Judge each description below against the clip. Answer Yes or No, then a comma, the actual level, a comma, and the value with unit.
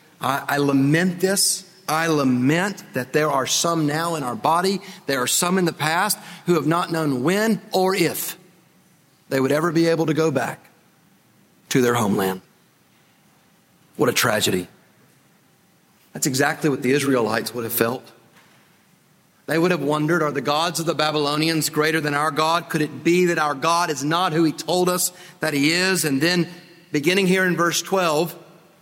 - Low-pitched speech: No, medium, 165 Hz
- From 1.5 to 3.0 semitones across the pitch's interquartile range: No, average, 3.4 semitones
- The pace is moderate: Yes, average, 175 wpm